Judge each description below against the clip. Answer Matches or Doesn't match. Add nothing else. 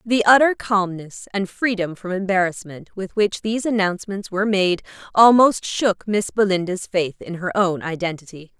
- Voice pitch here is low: Doesn't match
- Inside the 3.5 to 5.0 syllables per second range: Matches